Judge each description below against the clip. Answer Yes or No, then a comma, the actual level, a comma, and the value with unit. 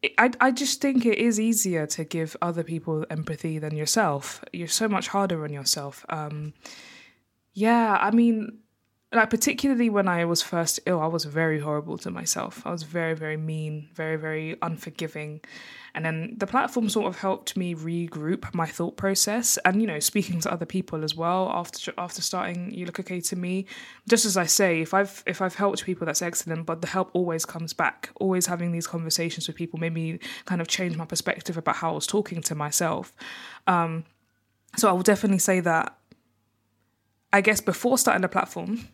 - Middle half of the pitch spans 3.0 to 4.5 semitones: Yes, average, 3.7 semitones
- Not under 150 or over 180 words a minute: No, average, 195 wpm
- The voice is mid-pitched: Yes, medium, 175 Hz